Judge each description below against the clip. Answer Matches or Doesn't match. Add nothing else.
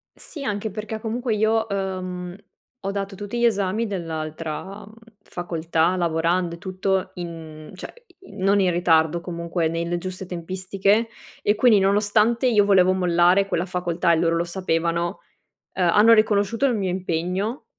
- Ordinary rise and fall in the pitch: Matches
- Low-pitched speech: Doesn't match